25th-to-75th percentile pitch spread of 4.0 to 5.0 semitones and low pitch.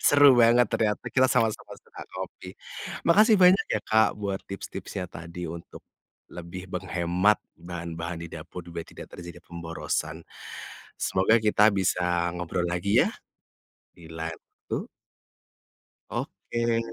Yes: average, 4.3 semitones; very low, 90 Hz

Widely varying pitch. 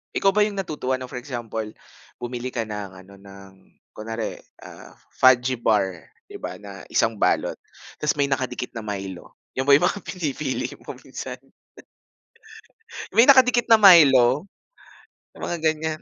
Yes: wide, 6.2 semitones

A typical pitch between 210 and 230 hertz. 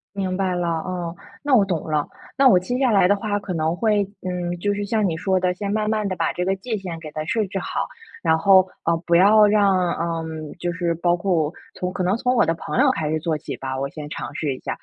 No: medium, 185 Hz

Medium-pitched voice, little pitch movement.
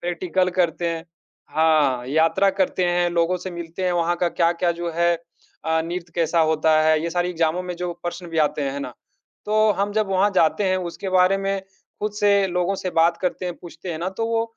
Yes: medium, 175 Hz; narrow, 2.1 semitones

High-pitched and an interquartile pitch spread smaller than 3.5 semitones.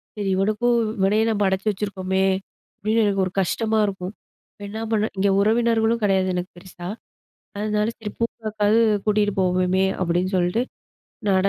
Yes: high, 205 Hz; narrow, 2.4 semitones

